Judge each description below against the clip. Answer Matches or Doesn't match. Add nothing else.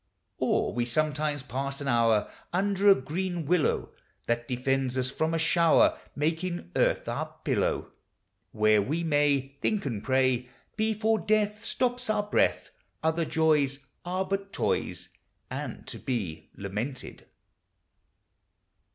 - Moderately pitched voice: Matches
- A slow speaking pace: Matches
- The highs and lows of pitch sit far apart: Matches